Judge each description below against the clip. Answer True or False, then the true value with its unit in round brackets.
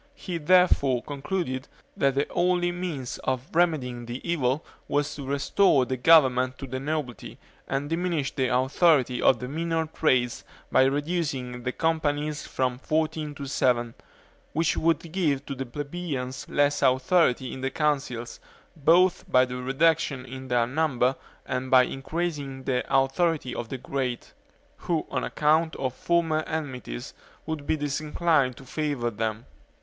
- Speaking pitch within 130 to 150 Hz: True (140 Hz)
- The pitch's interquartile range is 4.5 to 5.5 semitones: False (3.8 semitones)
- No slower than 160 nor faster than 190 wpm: False (145 wpm)